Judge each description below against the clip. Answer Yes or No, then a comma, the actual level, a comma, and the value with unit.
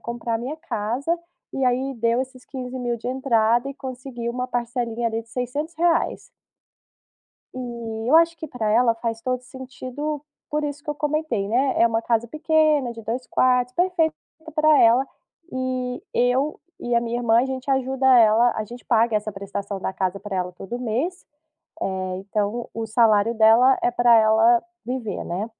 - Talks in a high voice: Yes, high, 245 Hz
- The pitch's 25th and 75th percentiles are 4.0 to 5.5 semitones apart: No, average, 2.8 semitones